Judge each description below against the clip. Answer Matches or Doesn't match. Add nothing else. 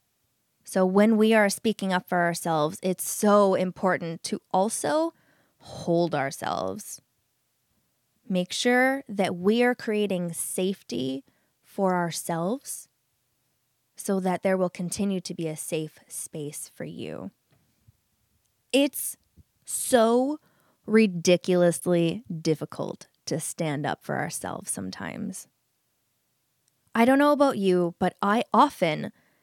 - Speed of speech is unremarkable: Doesn't match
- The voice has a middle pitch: Matches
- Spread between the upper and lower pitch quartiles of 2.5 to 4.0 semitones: Doesn't match